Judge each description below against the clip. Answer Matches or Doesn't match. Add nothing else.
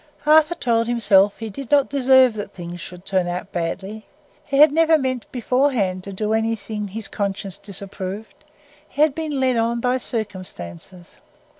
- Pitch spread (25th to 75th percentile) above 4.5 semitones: Matches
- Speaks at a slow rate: Doesn't match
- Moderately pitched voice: Doesn't match